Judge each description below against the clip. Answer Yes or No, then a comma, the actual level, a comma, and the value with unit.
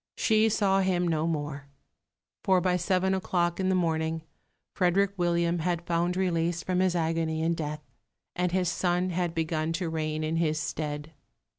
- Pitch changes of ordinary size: No, narrow, 2.2 semitones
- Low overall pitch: No, medium, 170 Hz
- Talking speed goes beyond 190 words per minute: No, average, 165 wpm